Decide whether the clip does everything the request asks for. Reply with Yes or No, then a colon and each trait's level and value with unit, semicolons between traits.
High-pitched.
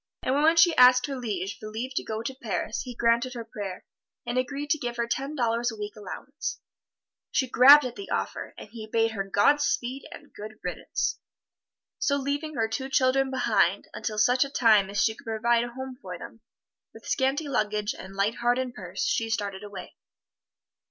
Yes: high, 240 Hz